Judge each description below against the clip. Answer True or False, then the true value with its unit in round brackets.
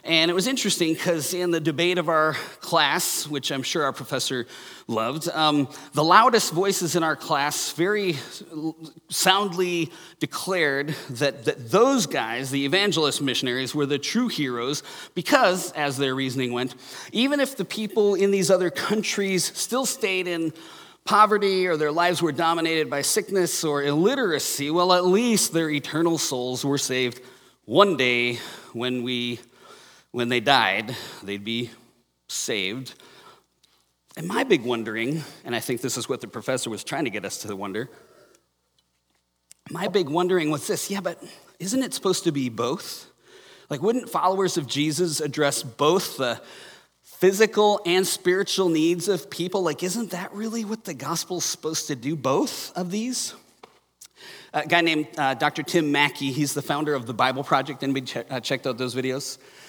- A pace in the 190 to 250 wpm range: False (165 wpm)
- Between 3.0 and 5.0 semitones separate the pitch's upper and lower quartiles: False (5.4 semitones)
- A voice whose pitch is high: False (155 Hz)